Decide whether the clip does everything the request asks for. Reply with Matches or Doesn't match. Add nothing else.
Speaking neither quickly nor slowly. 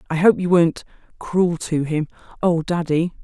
Matches